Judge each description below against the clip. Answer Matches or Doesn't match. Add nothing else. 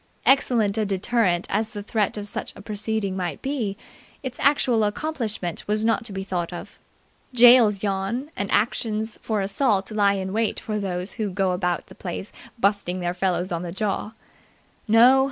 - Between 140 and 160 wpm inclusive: Doesn't match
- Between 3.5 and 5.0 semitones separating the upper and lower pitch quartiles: Doesn't match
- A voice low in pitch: Doesn't match